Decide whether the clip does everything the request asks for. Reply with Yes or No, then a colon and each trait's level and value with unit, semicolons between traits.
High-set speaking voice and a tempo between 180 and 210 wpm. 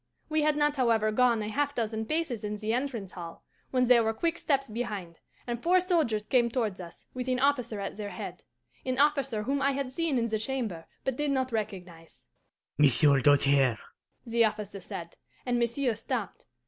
Yes: high, 235 Hz; average, 185 wpm